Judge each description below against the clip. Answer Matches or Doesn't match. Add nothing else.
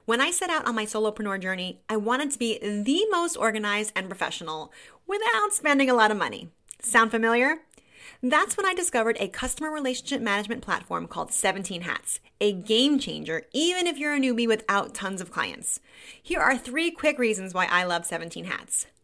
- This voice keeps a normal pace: Matches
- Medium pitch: Doesn't match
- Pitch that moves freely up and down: Matches